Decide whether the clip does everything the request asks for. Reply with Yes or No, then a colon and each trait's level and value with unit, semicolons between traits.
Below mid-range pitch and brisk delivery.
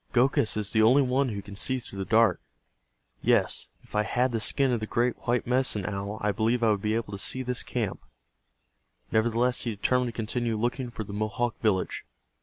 Yes: low, 115 Hz; fast, 210 wpm